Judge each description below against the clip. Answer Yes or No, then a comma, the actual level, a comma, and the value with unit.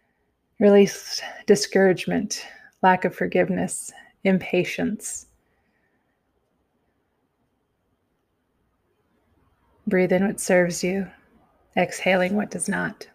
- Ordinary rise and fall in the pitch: No, narrow, 2.1 semitones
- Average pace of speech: No, slow, 70 wpm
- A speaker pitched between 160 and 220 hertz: Yes, high, 190 Hz